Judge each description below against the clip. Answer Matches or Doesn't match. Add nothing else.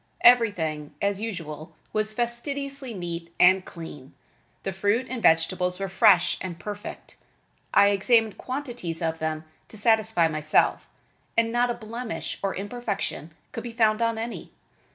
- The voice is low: Doesn't match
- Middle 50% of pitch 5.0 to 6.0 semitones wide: Matches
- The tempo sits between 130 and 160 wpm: Matches